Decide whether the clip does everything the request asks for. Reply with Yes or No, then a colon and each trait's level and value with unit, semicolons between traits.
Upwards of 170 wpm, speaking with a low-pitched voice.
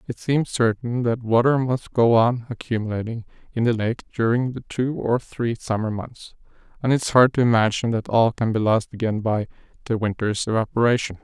Yes: average, 185 wpm; low, 115 Hz